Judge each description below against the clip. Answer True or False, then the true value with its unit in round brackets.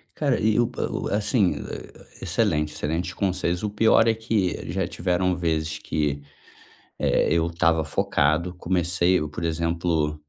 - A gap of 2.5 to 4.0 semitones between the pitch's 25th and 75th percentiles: True (3.6 semitones)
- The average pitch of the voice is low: True (85 Hz)